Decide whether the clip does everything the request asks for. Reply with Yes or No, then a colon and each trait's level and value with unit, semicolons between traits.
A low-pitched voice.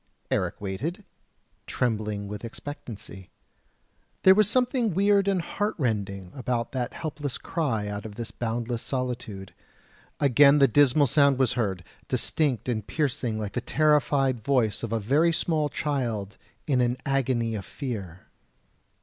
Yes: low, 125 Hz